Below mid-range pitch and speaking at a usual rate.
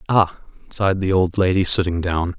Yes: very low, 90 Hz; average, 175 wpm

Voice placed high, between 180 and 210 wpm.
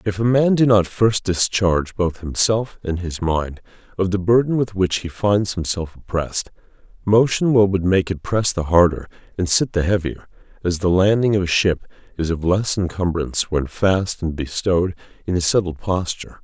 No: very low, 95 Hz; average, 185 wpm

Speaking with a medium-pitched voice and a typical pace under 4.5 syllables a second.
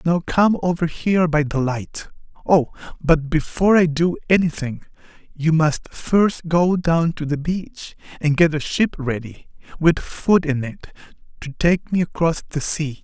Yes: medium, 160 Hz; 4.2 syllables/s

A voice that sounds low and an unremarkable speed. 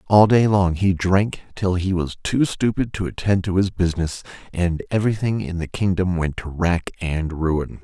Yes: very low, 90 Hz; average, 190 wpm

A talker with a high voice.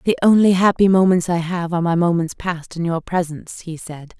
No: medium, 175 Hz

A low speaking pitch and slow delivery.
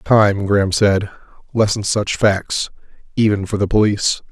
Yes: low, 100 Hz; slow, 125 wpm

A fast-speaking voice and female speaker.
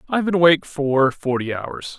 No: fast, 210 wpm; male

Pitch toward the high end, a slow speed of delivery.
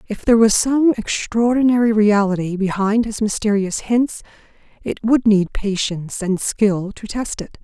No: high, 215 Hz; average, 150 wpm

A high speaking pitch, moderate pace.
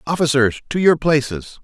No: medium, 140 Hz; average, 145 wpm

